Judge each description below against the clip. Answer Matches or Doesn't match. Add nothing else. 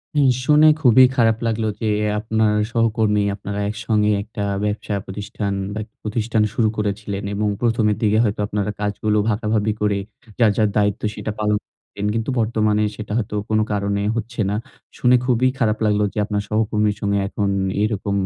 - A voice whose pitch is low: Matches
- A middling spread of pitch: Doesn't match